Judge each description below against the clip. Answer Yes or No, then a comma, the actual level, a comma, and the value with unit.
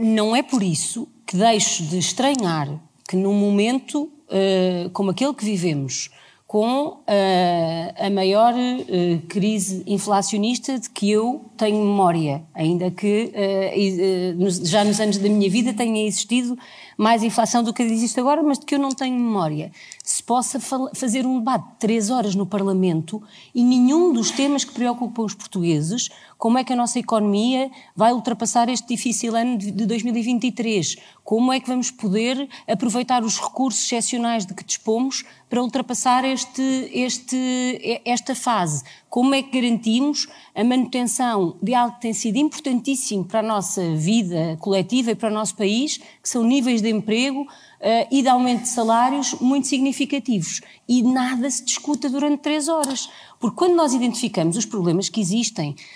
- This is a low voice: No, high, 230 Hz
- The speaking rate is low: No, average, 155 wpm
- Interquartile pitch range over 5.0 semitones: No, average, 4.0 semitones